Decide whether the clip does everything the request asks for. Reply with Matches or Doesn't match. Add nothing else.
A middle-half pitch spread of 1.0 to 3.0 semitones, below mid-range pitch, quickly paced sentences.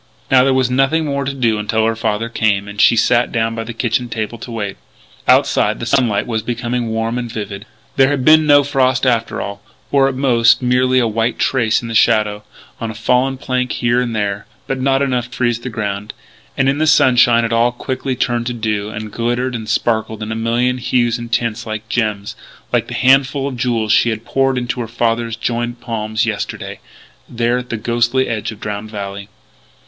Matches